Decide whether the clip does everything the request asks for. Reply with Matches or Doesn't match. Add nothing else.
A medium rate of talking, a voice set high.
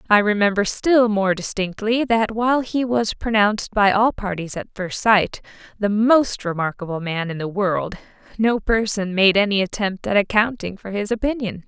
Matches